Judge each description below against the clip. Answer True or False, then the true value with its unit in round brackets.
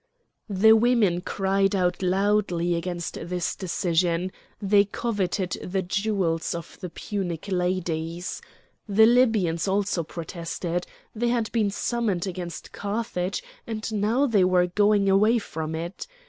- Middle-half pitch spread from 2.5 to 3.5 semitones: True (3.1 semitones)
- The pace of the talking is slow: True (125 wpm)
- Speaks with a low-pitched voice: False (190 Hz)